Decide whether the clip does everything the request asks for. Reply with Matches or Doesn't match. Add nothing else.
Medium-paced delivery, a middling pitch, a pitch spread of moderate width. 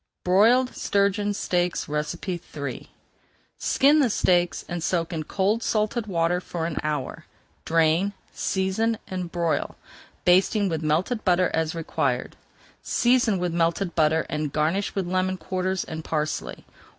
Doesn't match